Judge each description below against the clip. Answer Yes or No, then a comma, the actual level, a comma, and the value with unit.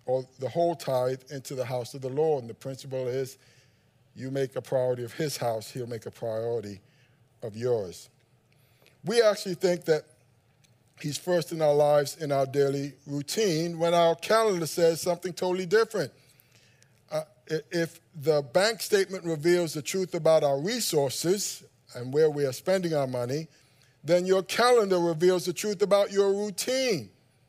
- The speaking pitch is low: No, medium, 145 Hz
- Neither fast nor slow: Yes, average, 160 wpm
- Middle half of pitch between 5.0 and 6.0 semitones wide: Yes, wide, 5.4 semitones